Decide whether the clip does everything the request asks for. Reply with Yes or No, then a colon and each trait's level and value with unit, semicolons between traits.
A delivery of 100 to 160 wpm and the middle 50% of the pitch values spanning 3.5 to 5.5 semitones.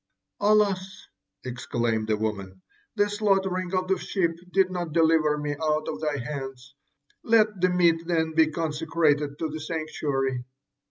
Yes: average, 145 wpm; average, 4.3 semitones